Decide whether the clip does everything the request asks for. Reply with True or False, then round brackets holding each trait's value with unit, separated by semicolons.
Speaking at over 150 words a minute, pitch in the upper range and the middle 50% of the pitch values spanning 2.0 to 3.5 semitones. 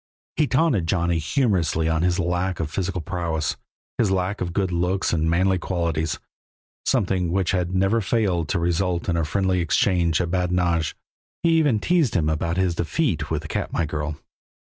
False (170 wpm; 90 Hz; 2.5 semitones)